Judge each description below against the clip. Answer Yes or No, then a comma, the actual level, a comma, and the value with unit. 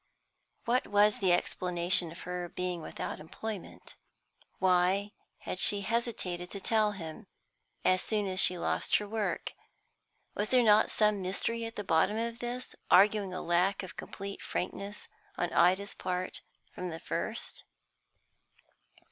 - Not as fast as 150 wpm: Yes, average, 140 wpm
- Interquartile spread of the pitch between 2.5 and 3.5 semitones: Yes, average, 2.8 semitones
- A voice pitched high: Yes, high, 195 Hz